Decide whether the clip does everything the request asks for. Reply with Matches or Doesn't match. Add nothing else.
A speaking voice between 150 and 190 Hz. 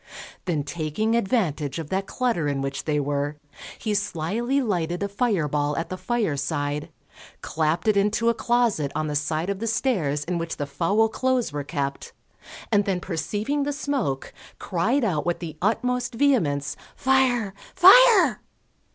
Matches